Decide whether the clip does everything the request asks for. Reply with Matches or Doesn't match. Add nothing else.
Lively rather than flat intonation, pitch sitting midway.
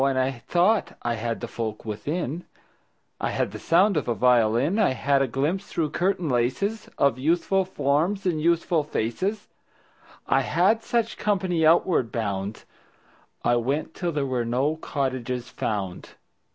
Matches